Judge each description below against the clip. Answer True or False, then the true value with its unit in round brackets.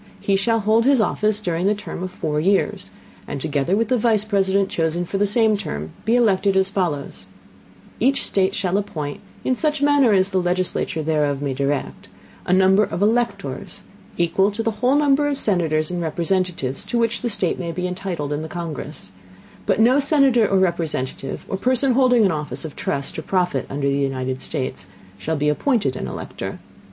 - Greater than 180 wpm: True (190 wpm)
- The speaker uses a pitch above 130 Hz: True (190 Hz)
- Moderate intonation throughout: False (5.9 semitones)